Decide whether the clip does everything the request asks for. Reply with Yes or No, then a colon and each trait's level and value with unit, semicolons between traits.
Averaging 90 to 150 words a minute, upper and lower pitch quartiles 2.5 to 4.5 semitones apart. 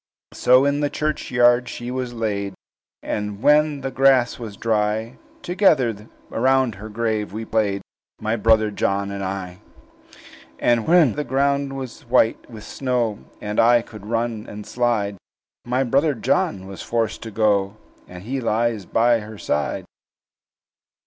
Yes: average, 145 wpm; average, 3.4 semitones